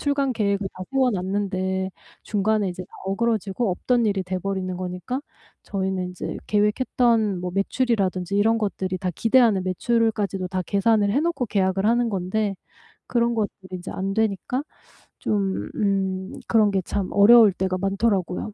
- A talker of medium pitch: No, high, 200 Hz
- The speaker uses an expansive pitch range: No, average, 3.1 semitones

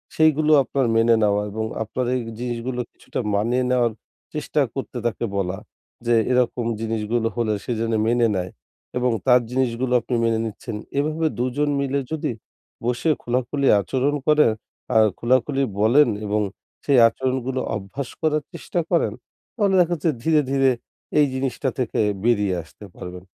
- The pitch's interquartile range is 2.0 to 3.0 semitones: No, average, 3.5 semitones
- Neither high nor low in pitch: No, low, 125 Hz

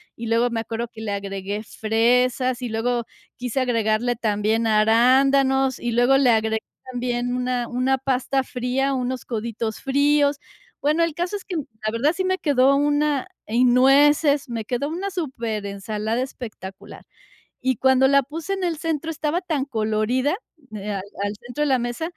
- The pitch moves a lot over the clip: No, average, 3.9 semitones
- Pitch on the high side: Yes, very high, 250 Hz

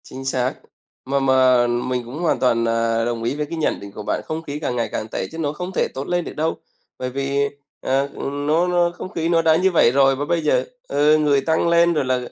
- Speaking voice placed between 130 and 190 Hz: Yes, medium, 140 Hz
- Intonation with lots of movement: No, average, 4.2 semitones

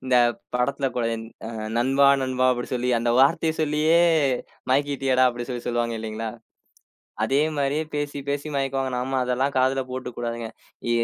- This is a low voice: Yes, low, 130 Hz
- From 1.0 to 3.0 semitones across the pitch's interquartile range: Yes, narrow, 2.4 semitones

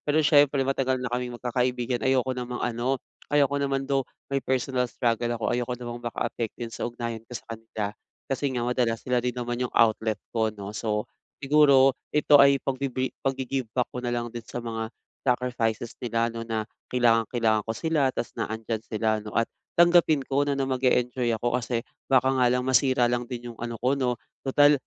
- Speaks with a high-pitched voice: No, low, 125 Hz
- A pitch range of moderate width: No, narrow, 2.3 semitones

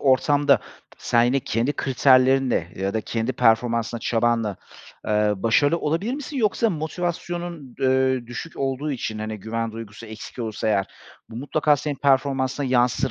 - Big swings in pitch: No, average, 4.0 semitones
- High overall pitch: No, low, 130 Hz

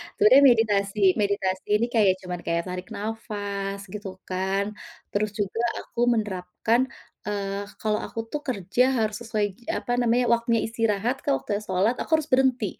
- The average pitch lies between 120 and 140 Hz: No, high, 210 Hz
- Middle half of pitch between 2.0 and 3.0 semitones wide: Yes, average, 2.7 semitones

